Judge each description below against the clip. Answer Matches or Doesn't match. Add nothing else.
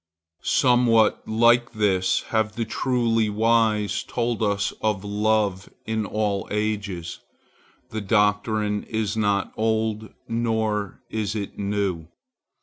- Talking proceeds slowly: Matches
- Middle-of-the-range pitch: Doesn't match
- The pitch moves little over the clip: Matches